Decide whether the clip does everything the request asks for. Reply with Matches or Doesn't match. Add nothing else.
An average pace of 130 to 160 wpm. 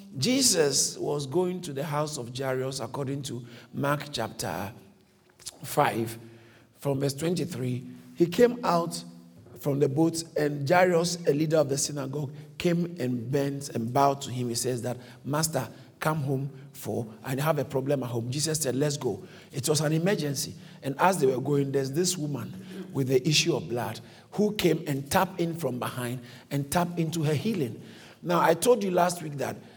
Doesn't match